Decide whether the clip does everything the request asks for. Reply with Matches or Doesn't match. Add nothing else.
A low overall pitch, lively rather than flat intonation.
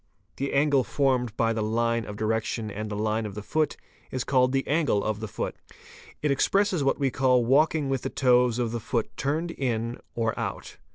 Doesn't match